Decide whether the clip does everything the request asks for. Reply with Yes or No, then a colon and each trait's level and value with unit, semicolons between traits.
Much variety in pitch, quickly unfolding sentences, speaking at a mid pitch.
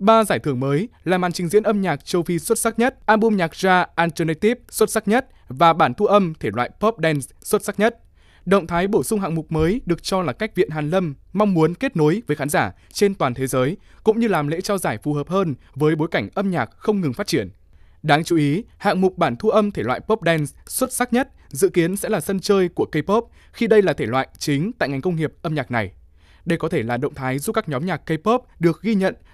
Yes: wide, 5.7 semitones; fast, 260 wpm; medium, 175 Hz